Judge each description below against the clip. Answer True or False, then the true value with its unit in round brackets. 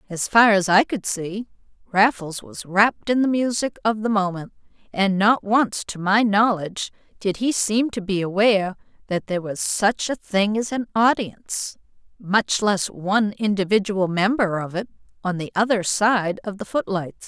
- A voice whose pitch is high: True (205 Hz)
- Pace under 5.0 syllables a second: True (4.5 syllables/s)